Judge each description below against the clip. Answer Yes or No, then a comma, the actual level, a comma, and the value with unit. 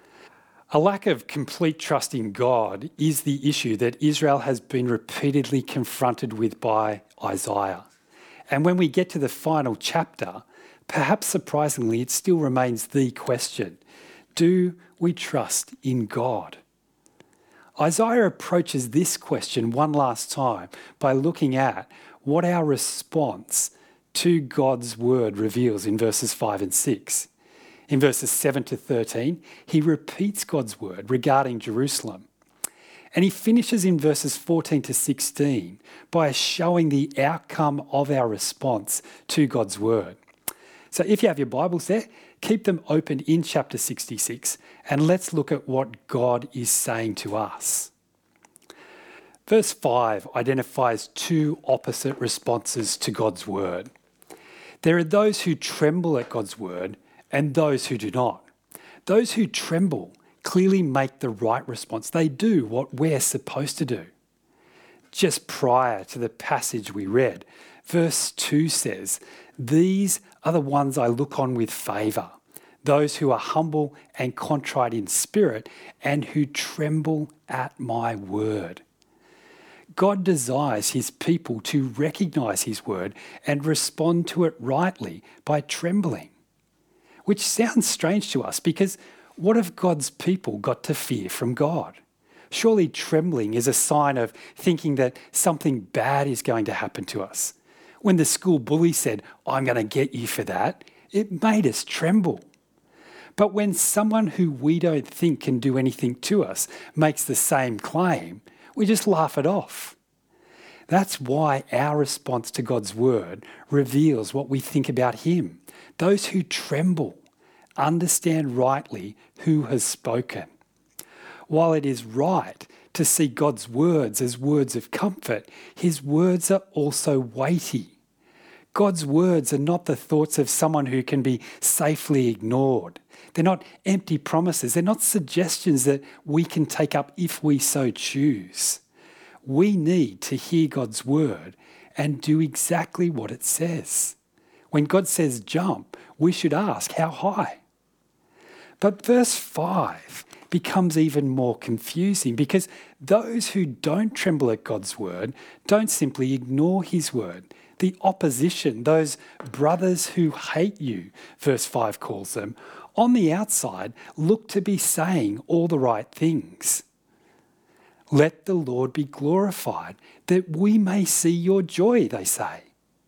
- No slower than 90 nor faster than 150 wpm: Yes, average, 140 wpm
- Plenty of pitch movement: No, average, 4.9 semitones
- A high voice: No, medium, 150 Hz